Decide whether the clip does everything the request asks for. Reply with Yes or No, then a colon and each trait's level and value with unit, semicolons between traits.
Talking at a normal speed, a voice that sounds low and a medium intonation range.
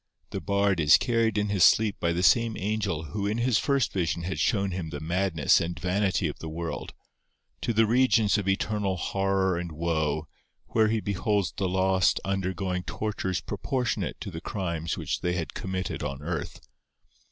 Yes: average, 175 wpm; very low, 95 Hz; average, 3.6 semitones